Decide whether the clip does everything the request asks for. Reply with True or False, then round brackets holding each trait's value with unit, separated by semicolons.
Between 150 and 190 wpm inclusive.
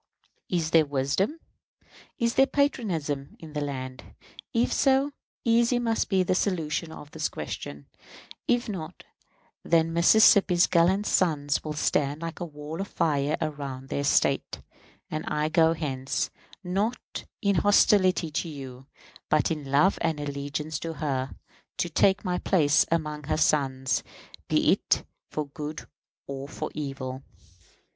False (140 wpm)